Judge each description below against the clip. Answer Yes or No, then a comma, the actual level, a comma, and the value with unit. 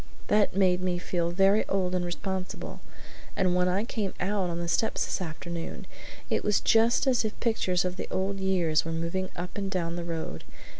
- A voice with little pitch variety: Yes, narrow, 2.2 semitones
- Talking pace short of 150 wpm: No, average, 195 wpm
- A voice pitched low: No, medium, 185 Hz